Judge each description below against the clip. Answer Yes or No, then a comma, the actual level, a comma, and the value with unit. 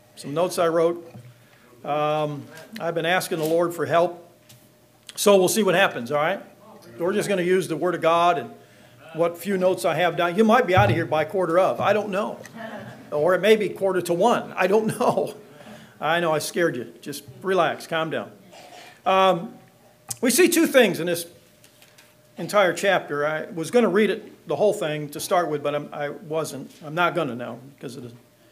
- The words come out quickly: Yes, fast, 210 wpm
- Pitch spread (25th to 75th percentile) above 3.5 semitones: Yes, average, 4.0 semitones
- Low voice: No, medium, 170 Hz